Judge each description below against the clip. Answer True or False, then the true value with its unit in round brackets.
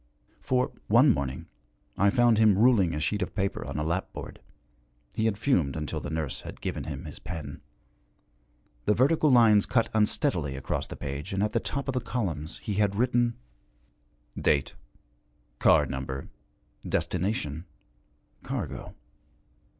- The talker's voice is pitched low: True (100 Hz)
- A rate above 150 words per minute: False (145 wpm)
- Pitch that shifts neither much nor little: False (7.5 semitones)